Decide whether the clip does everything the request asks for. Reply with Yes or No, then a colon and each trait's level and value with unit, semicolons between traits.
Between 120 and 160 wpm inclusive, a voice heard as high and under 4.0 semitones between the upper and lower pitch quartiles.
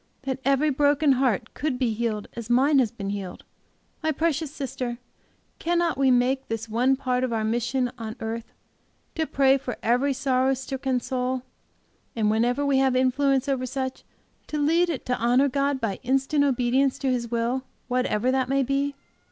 No: average, 175 wpm; very high, 260 Hz; narrow, 2.4 semitones